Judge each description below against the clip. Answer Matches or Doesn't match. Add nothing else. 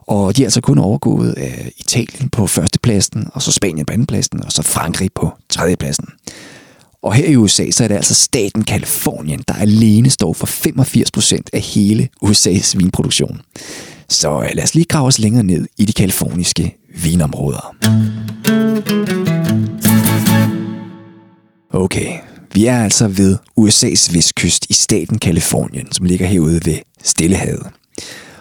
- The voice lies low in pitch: Matches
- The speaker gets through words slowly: Matches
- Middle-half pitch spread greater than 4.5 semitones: Doesn't match